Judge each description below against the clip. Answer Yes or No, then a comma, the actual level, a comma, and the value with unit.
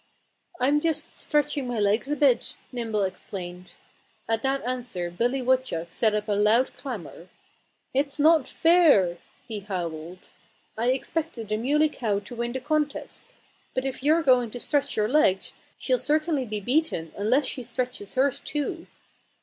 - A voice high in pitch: Yes, very high, 250 Hz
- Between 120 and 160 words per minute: Yes, average, 155 wpm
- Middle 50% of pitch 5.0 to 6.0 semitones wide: Yes, wide, 5.5 semitones